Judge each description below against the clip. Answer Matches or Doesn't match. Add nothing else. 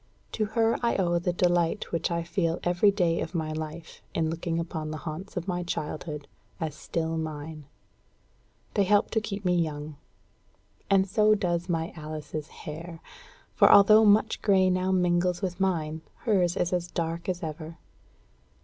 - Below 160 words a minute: Doesn't match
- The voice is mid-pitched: Matches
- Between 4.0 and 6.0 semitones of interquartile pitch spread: Doesn't match